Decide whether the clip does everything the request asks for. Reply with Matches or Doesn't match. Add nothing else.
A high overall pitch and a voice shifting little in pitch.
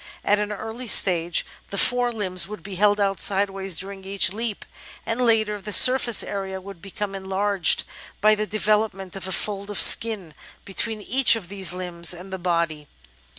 Matches